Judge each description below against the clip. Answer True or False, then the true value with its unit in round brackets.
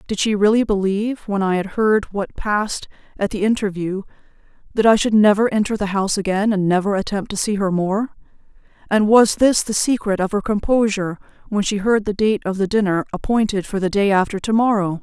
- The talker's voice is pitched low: False (205 Hz)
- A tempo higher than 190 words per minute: True (205 wpm)